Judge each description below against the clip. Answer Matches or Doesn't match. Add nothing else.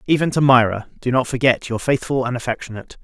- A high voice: Doesn't match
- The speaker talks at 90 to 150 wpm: Doesn't match